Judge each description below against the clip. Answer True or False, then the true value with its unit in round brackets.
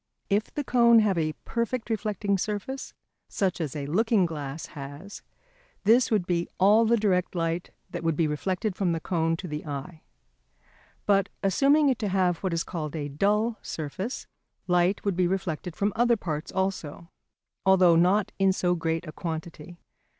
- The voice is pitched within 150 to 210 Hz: True (185 Hz)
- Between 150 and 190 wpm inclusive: True (170 wpm)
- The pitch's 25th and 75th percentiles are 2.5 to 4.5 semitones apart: True (4.1 semitones)